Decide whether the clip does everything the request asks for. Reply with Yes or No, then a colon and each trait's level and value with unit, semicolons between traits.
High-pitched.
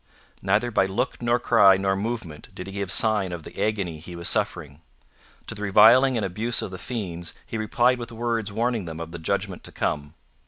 No: low, 100 Hz